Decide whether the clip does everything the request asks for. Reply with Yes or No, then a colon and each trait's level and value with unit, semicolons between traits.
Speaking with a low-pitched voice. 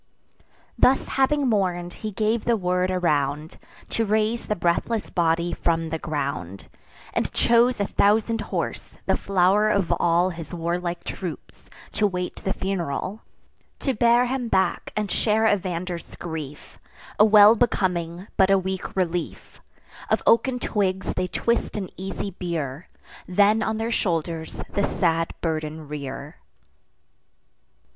No: medium, 185 Hz